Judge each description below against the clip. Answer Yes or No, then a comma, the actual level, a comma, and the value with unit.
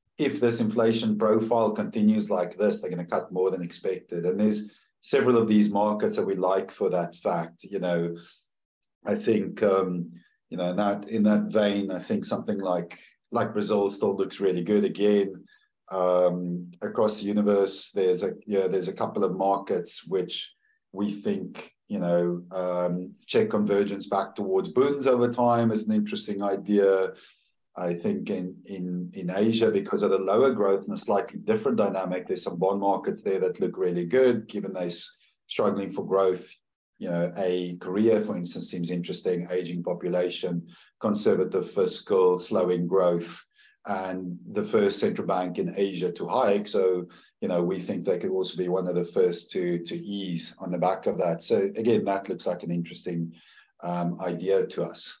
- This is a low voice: Yes, very low, 95 Hz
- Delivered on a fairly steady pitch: No, average, 3.1 semitones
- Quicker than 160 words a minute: Yes, average, 180 wpm